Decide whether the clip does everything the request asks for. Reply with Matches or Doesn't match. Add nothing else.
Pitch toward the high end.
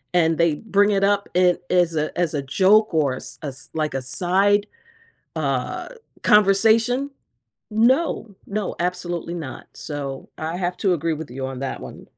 Doesn't match